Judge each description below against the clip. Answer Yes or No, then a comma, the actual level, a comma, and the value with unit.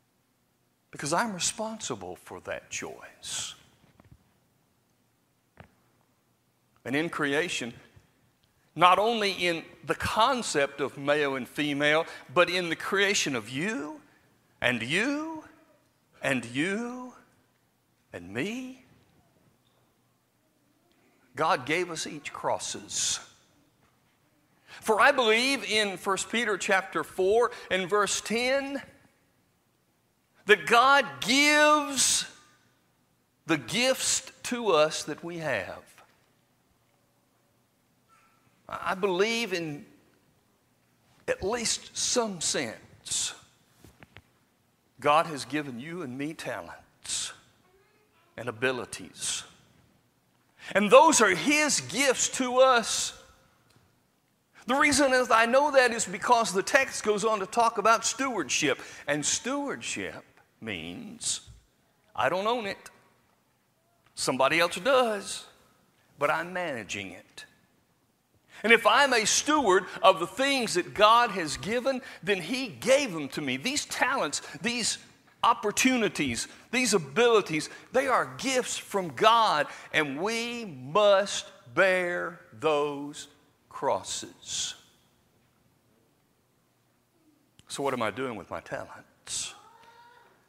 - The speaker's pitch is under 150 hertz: No, high, 210 Hz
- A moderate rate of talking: No, slow, 100 wpm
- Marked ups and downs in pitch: Yes, wide, 7.4 semitones